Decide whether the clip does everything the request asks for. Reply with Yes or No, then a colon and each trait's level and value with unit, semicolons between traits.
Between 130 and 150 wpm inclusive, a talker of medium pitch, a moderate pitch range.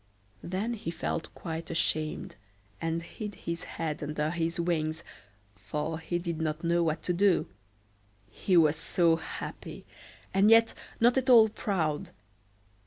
Yes: average, 140 wpm; medium, 170 Hz; average, 3.0 semitones